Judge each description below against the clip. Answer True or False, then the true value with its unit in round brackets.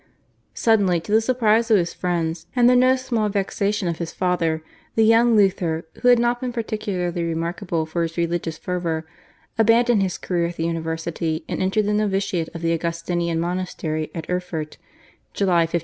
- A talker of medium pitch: True (180 Hz)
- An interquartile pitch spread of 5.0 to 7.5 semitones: False (4.3 semitones)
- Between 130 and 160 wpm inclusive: False (175 wpm)